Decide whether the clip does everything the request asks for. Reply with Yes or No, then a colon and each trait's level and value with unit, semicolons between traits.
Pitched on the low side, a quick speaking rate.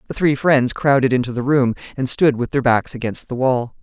Yes: low, 130 Hz; fast, 235 wpm